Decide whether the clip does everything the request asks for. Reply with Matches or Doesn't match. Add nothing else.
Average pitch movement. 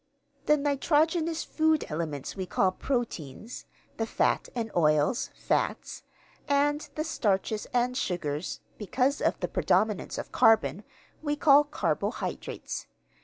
Doesn't match